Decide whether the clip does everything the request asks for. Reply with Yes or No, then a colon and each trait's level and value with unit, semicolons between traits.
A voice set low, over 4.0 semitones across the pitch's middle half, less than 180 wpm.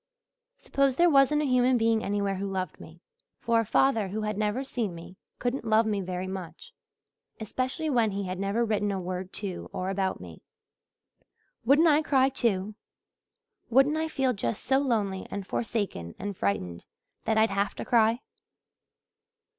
No: high, 215 Hz; average, 5.0 semitones; average, 165 wpm